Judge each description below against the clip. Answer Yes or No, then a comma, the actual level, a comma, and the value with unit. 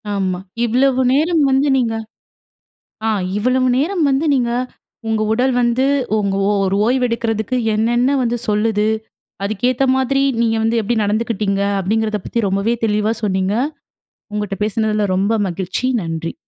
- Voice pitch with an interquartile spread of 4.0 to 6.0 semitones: No, average, 3.5 semitones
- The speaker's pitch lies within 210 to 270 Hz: Yes, high, 225 Hz